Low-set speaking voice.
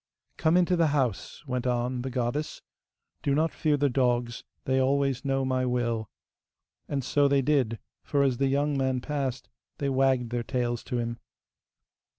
Yes: low, 130 Hz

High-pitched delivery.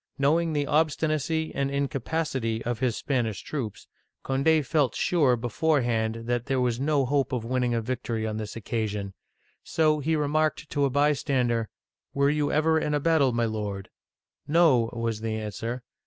No: low, 130 Hz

